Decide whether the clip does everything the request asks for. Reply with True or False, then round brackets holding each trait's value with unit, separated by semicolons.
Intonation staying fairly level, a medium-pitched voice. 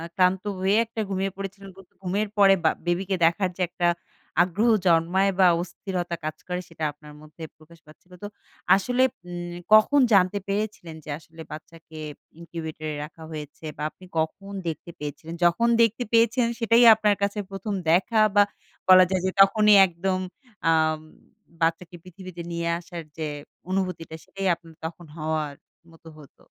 False (3.2 semitones; 180 Hz)